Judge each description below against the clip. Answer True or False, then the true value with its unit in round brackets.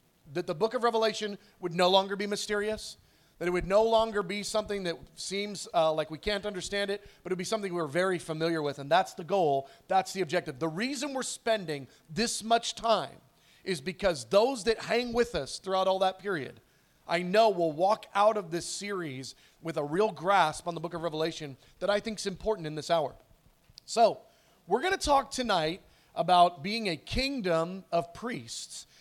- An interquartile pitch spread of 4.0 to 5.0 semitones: True (4.4 semitones)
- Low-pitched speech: False (190 Hz)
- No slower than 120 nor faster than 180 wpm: False (195 wpm)